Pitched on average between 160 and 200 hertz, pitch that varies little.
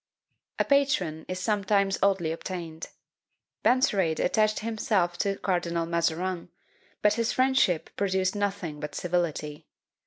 No: medium, 185 Hz; average, 3.5 semitones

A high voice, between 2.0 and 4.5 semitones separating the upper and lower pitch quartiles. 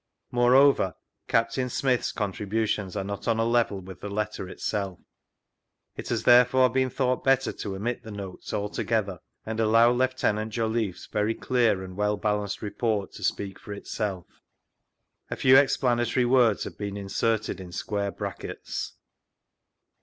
No: low, 110 Hz; average, 3.2 semitones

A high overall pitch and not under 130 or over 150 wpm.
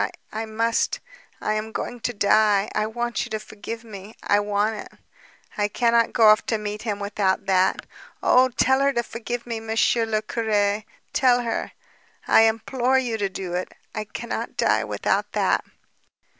No: high, 220 Hz; average, 170 wpm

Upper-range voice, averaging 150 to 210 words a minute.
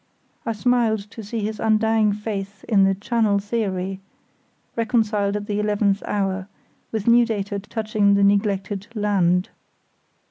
No: high, 205 Hz; slow, 135 wpm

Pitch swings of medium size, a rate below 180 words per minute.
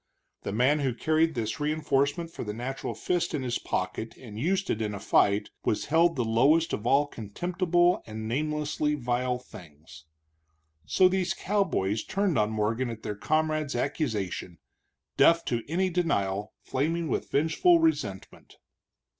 No: wide, 7.0 semitones; average, 155 wpm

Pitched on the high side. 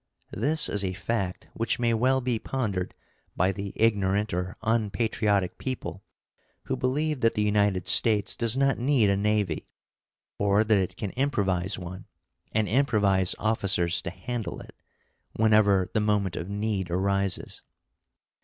No: low, 105 Hz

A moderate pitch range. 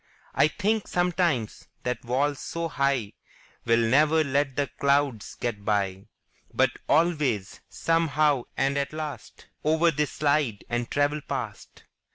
Yes: average, 4.2 semitones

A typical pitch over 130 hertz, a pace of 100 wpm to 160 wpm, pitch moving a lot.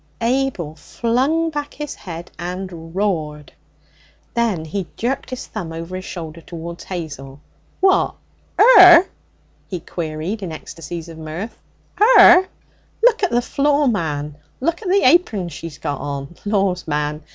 Yes: medium, 185 Hz; average, 140 wpm; wide, 8.9 semitones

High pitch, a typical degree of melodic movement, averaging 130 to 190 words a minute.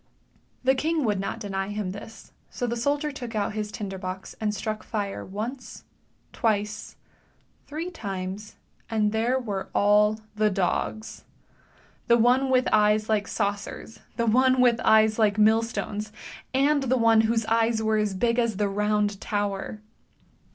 No: high, 215 Hz; narrow, 2.3 semitones; average, 150 wpm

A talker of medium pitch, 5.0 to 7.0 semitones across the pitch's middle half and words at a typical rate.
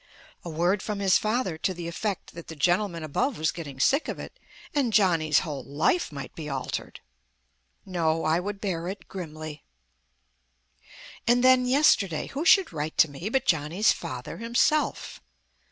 Yes: medium, 175 Hz; wide, 5.6 semitones; average, 160 wpm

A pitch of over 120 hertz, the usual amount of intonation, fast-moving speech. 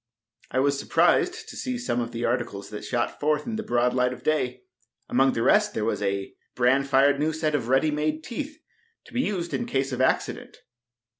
Yes: low, 135 Hz; average, 4.1 semitones; fast, 210 wpm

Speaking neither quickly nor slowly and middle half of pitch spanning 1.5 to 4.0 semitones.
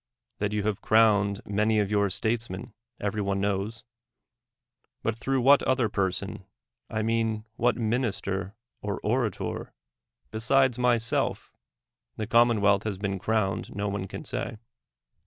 No: slow, 130 wpm; narrow, 2.4 semitones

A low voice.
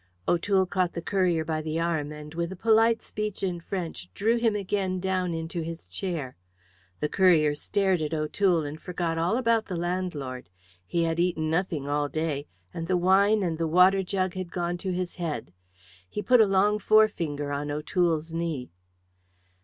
No: medium, 175 Hz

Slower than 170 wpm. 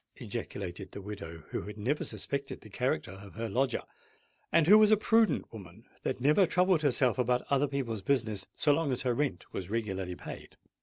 No: average, 190 wpm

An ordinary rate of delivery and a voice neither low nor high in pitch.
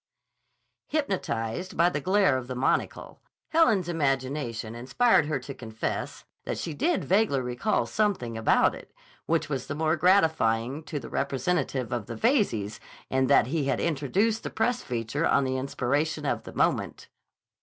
Yes: average, 155 wpm; medium, 145 Hz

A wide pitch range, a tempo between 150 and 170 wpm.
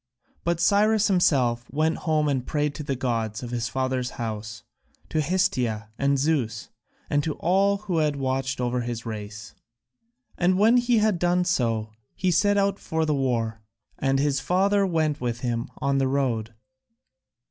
Yes: wide, 6.6 semitones; average, 165 wpm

